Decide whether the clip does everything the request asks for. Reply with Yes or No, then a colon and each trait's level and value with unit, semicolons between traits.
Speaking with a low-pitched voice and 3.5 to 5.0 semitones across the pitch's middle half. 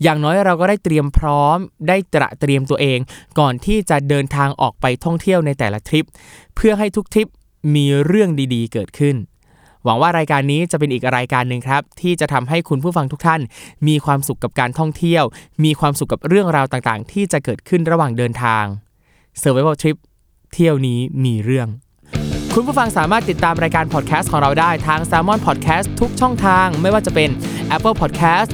No: medium, 150 Hz; average, 4.5 semitones